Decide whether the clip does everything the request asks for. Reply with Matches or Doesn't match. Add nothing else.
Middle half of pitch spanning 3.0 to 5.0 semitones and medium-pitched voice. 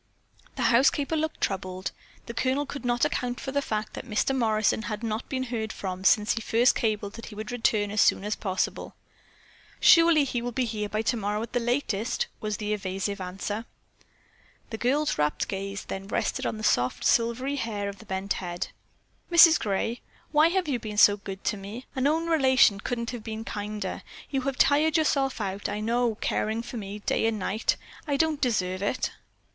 Doesn't match